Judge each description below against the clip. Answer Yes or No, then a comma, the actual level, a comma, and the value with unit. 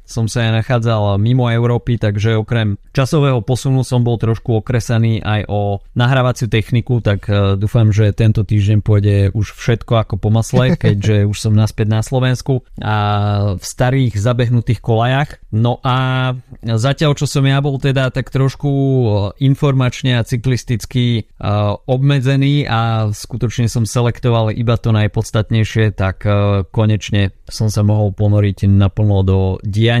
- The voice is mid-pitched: No, low, 115 Hz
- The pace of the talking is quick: No, average, 140 wpm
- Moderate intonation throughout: Yes, average, 3.1 semitones